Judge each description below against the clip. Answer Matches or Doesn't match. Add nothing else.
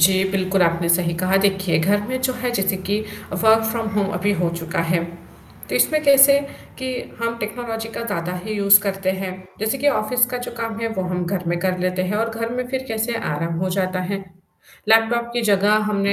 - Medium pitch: Doesn't match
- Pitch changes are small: Doesn't match